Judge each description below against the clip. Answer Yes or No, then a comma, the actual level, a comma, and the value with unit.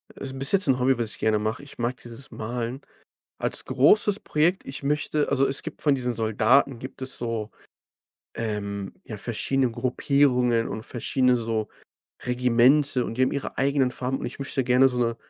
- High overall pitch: No, low, 125 Hz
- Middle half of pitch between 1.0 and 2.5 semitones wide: No, average, 2.9 semitones